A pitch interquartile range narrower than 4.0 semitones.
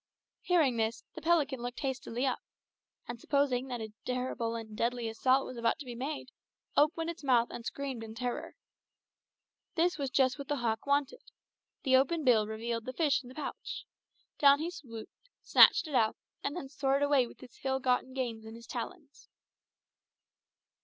Yes: average, 3.3 semitones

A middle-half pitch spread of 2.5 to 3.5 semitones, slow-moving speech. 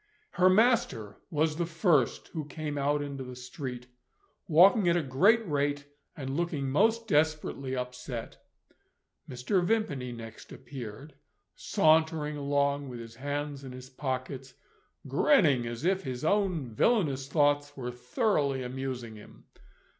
No: average, 4.1 semitones; slow, 130 wpm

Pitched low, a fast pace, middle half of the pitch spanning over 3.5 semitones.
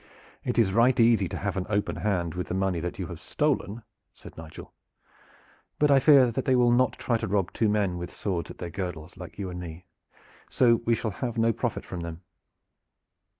Yes: low, 100 Hz; fast, 210 wpm; average, 4.9 semitones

